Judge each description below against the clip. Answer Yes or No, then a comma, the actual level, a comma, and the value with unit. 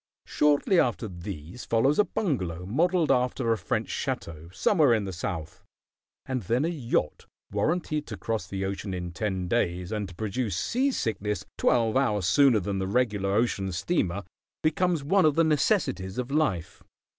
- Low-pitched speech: Yes, low, 110 Hz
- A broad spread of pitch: Yes, wide, 7.3 semitones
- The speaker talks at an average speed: Yes, average, 165 wpm